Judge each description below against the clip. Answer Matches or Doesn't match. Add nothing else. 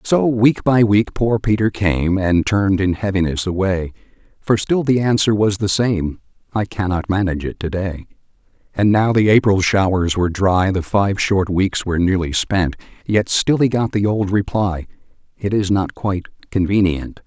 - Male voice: Matches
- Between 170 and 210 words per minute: Matches